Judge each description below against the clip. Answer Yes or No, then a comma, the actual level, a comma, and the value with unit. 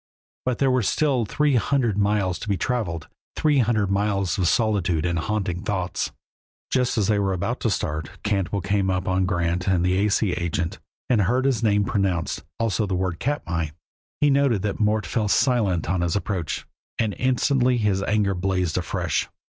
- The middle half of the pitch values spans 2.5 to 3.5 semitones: No, average, 4.0 semitones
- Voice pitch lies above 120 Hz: No, low, 100 Hz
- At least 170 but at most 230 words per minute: Yes, average, 180 wpm